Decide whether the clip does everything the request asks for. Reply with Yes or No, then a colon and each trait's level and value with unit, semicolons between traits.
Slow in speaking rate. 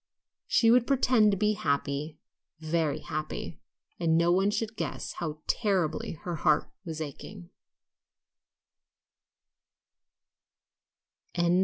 Yes: slow, 100 wpm